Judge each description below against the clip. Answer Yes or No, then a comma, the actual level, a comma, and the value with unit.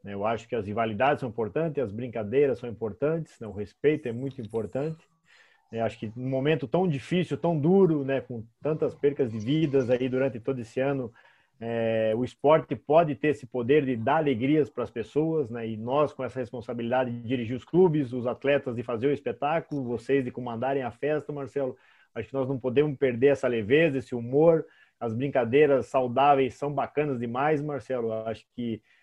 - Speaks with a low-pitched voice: Yes, low, 130 Hz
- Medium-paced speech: No, fast, 190 wpm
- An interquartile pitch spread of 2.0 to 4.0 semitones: Yes, average, 3.4 semitones